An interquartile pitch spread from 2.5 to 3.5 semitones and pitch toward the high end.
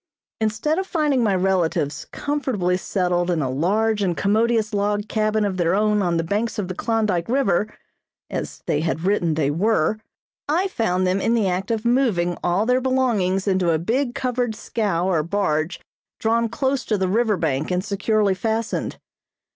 No: average, 4.2 semitones; high, 205 Hz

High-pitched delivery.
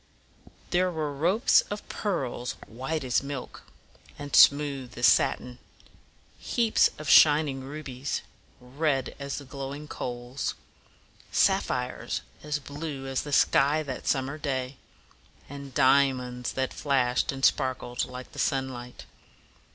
No: low, 135 Hz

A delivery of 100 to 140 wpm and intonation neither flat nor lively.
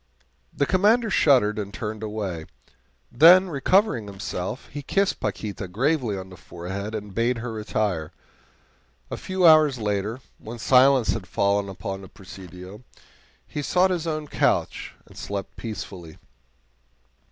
No: slow, 135 wpm; wide, 6.7 semitones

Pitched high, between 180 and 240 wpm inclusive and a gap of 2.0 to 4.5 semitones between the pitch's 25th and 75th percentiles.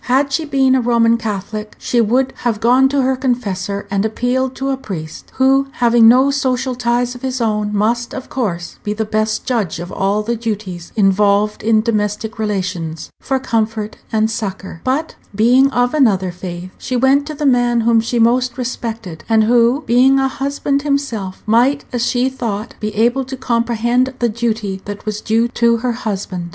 Yes: high, 235 Hz; average, 185 wpm; average, 3.4 semitones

